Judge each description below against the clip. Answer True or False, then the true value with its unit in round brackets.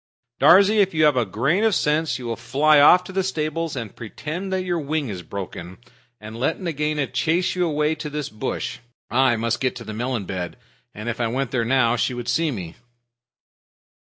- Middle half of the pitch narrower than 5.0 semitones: False (5.5 semitones)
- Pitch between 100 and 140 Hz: True (135 Hz)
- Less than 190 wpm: False (200 wpm)